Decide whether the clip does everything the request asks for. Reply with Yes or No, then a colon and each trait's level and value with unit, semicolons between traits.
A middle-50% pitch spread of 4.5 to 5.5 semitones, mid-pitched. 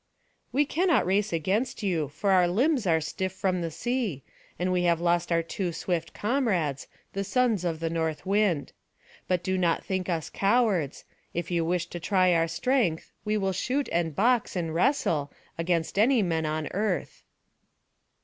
No: average, 4.1 semitones; medium, 180 Hz